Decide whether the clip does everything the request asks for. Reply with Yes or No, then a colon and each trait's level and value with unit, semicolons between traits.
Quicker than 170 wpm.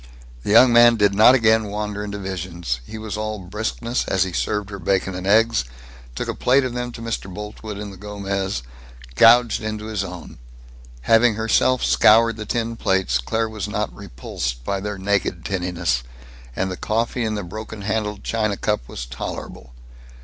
Yes: average, 180 wpm